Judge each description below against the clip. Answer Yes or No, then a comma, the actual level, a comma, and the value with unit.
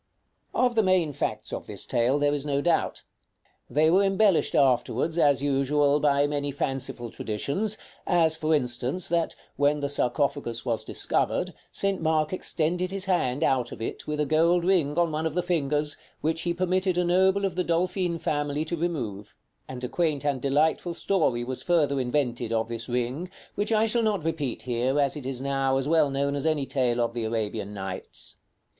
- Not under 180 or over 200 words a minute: Yes, average, 190 wpm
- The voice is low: No, medium, 145 Hz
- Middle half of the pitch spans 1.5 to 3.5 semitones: No, average, 4.6 semitones